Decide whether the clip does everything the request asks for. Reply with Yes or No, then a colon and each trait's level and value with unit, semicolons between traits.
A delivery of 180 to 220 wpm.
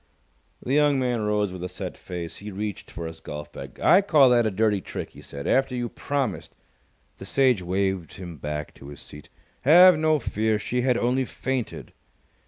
Yes: average, 195 wpm